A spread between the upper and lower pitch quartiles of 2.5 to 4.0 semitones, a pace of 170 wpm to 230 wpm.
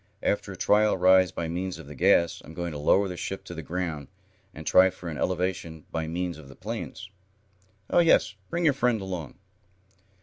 Yes: average, 2.8 semitones; average, 200 wpm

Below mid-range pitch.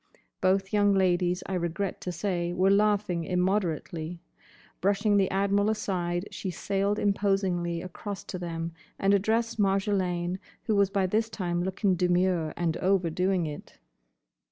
No: high, 190 Hz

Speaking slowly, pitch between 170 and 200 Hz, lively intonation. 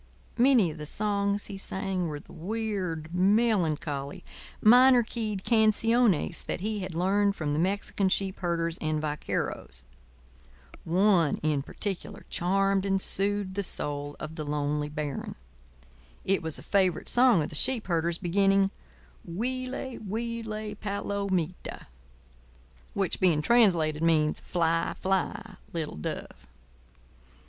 No: slow, 125 wpm; high, 190 Hz; average, 4.5 semitones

